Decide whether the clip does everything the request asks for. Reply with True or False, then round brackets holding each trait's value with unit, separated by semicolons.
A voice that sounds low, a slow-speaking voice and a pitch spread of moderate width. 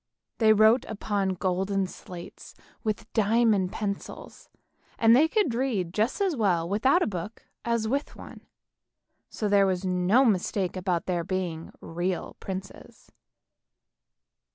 False (200 Hz; 125 wpm; 3.6 semitones)